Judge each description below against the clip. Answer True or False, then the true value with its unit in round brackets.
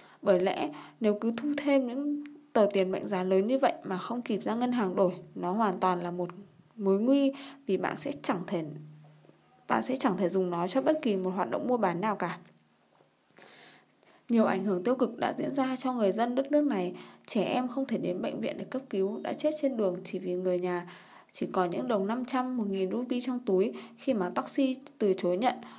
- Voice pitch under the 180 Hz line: False (210 Hz)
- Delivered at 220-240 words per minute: True (225 wpm)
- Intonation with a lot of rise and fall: True (5.9 semitones)